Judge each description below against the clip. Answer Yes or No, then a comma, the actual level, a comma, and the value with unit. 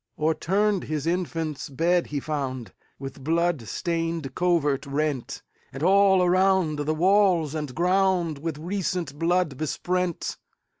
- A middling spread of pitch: Yes, average, 3.5 semitones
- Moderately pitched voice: Yes, medium, 165 Hz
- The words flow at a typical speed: No, slow, 105 wpm